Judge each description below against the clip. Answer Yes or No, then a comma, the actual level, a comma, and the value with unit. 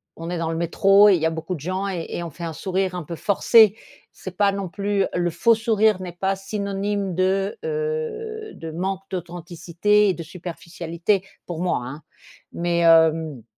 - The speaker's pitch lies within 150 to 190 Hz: Yes, medium, 185 Hz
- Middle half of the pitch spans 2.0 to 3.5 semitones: Yes, average, 3.0 semitones